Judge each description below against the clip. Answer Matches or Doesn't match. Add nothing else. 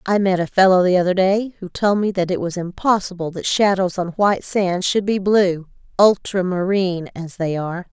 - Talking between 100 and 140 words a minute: Doesn't match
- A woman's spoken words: Matches